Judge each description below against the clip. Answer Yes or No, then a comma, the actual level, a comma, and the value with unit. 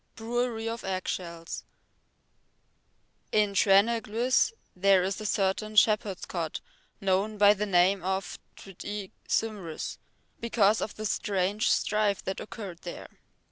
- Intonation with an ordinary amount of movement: No, narrow, 2.3 semitones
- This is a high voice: Yes, high, 200 Hz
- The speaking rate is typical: No, slow, 125 wpm